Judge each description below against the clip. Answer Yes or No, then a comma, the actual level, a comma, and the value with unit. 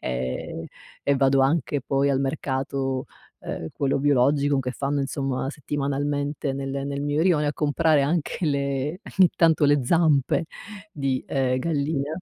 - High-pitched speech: No, medium, 140 Hz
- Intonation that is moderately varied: No, narrow, 1.5 semitones